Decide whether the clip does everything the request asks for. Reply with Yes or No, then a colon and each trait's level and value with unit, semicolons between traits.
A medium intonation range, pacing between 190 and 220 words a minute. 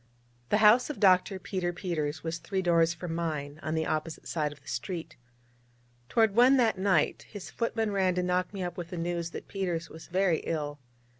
Yes: average, 3.1 semitones; average, 200 wpm